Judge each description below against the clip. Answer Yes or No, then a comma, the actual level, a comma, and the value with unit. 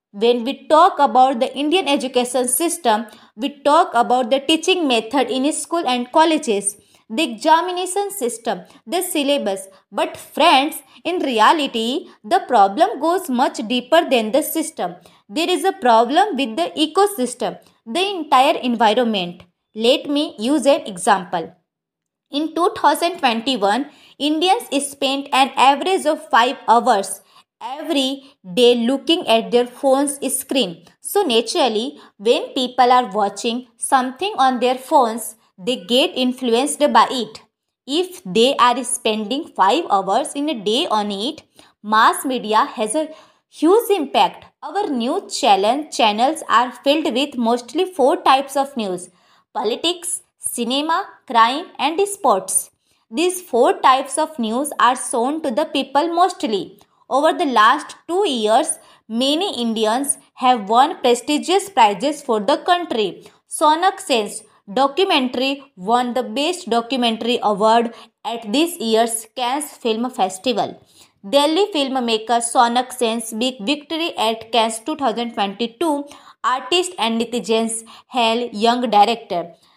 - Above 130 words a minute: No, average, 125 wpm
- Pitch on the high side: Yes, very high, 265 Hz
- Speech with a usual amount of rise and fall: Yes, average, 4.9 semitones